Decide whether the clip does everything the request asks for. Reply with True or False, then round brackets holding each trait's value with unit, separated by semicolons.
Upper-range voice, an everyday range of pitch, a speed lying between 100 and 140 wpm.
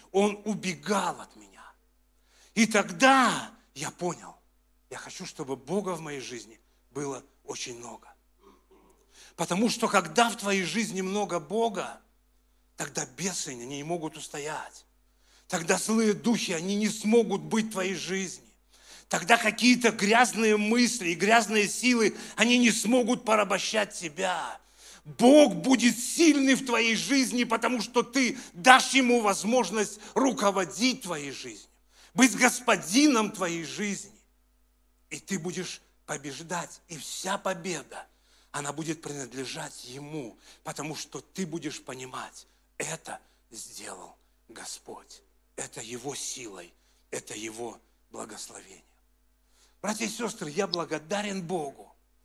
False (195 Hz; 6.4 semitones; 120 wpm)